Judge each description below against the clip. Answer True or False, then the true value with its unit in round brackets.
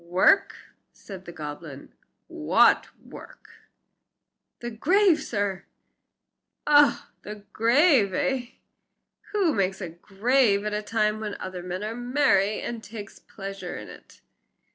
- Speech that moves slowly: True (120 wpm)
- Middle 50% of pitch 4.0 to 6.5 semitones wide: True (4.4 semitones)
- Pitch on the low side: False (210 Hz)